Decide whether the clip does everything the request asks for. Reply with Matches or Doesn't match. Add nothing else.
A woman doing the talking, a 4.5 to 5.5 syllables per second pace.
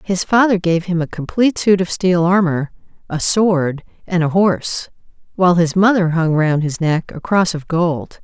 Matches